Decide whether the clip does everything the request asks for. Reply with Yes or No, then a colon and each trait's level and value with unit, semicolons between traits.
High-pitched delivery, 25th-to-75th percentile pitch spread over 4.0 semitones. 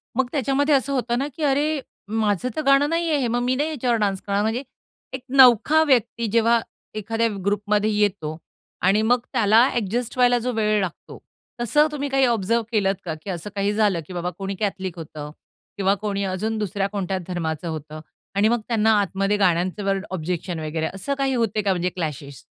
Yes: high, 210 Hz; average, 4.5 semitones